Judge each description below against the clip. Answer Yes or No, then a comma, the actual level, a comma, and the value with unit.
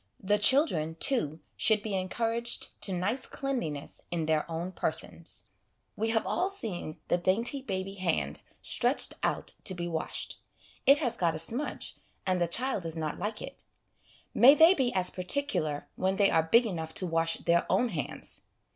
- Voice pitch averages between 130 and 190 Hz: Yes, medium, 185 Hz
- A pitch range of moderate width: No, wide, 6.3 semitones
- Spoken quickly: No, average, 175 wpm